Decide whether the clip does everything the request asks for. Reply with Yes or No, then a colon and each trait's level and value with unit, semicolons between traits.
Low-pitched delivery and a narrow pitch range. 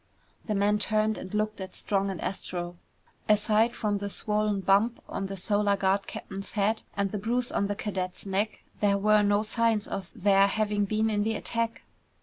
No: high, 205 Hz; narrow, 1.4 semitones